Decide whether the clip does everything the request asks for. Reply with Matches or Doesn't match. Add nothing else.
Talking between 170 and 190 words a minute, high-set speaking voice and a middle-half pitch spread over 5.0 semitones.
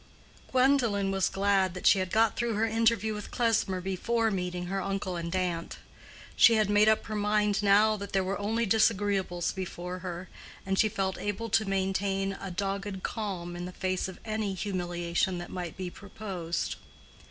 Doesn't match